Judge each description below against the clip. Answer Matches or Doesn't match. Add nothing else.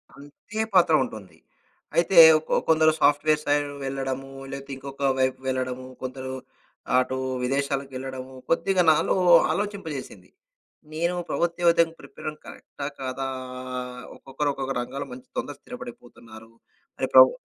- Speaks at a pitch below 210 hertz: Matches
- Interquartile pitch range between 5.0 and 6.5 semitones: Doesn't match